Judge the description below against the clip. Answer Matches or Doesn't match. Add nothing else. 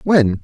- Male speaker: Matches